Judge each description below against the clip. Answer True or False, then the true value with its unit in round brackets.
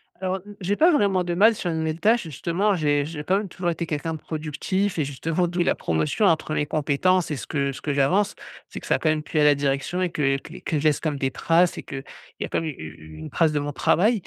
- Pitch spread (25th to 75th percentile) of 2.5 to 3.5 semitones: False (4.0 semitones)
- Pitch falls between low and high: True (160 Hz)